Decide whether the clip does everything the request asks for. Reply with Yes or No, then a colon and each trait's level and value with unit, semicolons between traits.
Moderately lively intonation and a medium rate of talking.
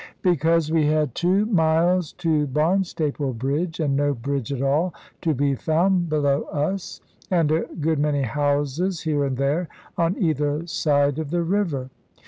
Yes: average, 3.1 semitones; average, 155 wpm